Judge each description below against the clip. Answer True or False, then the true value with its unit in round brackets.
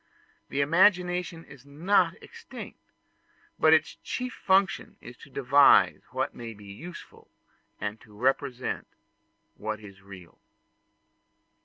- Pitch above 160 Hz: False (140 Hz)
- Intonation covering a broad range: True (8.8 semitones)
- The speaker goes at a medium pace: False (115 wpm)